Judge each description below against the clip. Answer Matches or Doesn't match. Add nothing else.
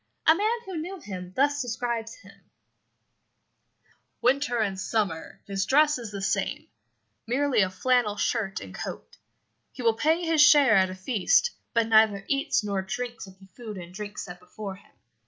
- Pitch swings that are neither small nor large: Doesn't match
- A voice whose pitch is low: Doesn't match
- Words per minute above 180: Doesn't match